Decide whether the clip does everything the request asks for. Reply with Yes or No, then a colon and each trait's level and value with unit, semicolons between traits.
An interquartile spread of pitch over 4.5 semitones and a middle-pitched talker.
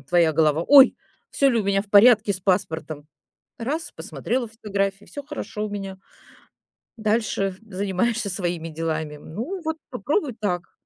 No: average, 5.0 semitones; high, 200 Hz